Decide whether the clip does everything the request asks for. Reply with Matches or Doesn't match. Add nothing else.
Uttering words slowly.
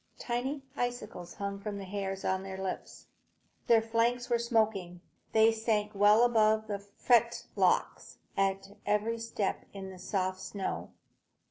Matches